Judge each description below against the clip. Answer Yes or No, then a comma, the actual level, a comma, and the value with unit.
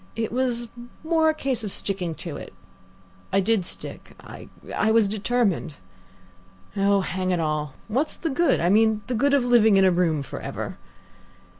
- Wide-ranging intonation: No, average, 4.9 semitones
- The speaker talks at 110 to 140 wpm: No, average, 175 wpm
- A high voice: Yes, high, 215 Hz